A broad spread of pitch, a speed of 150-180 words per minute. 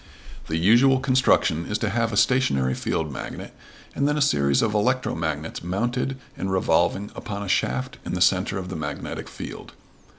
Yes: wide, 7.5 semitones; average, 170 wpm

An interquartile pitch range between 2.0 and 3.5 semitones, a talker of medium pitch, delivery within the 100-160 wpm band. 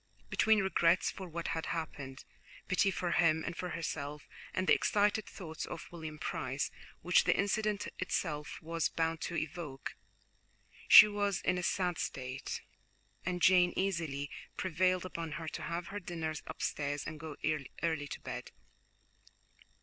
Yes: average, 2.9 semitones; medium, 170 Hz; average, 150 wpm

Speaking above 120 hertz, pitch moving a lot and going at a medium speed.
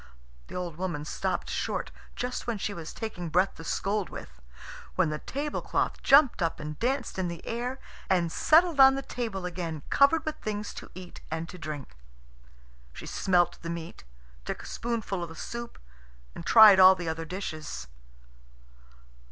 Yes: medium, 185 Hz; wide, 6.2 semitones; average, 170 wpm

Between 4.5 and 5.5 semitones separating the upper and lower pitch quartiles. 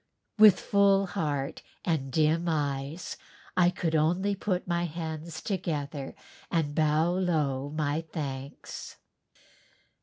No: average, 3.4 semitones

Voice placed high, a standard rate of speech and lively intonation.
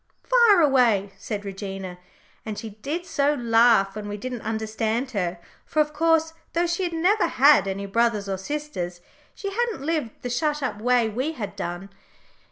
Yes: high, 235 Hz; average, 175 wpm; wide, 7.0 semitones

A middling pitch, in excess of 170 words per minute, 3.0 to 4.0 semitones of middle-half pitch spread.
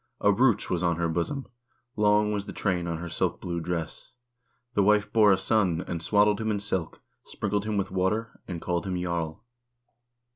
No: very low, 95 Hz; average, 190 wpm; average, 3.4 semitones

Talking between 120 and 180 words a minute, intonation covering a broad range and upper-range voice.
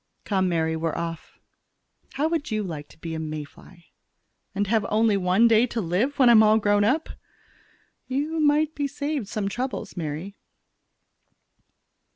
Yes: average, 160 wpm; wide, 7.2 semitones; high, 210 Hz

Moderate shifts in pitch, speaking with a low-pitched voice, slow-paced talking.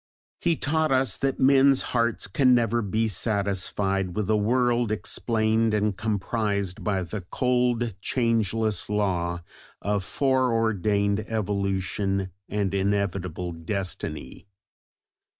Yes: average, 3.2 semitones; low, 105 Hz; slow, 105 wpm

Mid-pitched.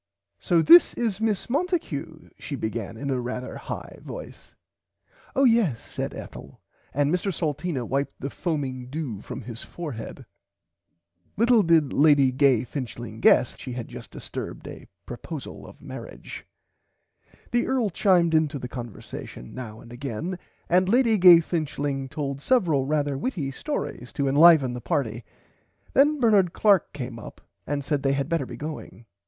Yes: medium, 145 Hz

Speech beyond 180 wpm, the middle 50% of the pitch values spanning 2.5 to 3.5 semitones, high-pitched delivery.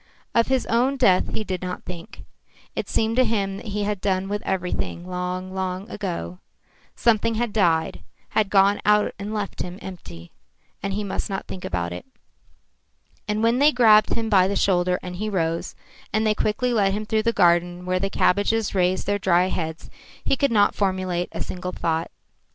Yes: average, 190 wpm; average, 2.9 semitones; high, 195 Hz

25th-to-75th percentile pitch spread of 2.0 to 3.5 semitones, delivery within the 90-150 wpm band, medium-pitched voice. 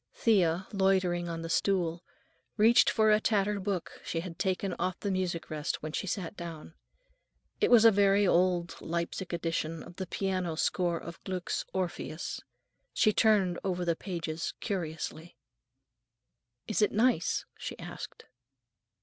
Yes: average, 2.8 semitones; average, 145 wpm; medium, 180 Hz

